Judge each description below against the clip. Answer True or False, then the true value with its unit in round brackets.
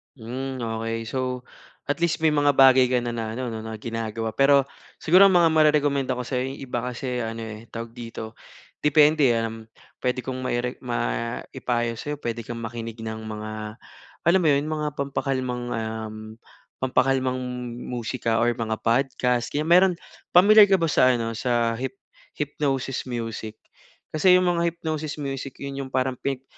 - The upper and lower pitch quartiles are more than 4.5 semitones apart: False (3.7 semitones)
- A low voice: True (125 Hz)